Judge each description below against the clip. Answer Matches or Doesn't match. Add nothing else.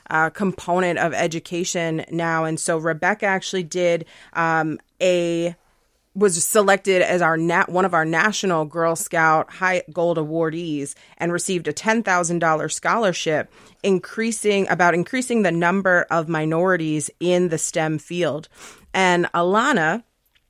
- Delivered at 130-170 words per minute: Matches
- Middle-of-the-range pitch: Matches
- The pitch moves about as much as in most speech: Doesn't match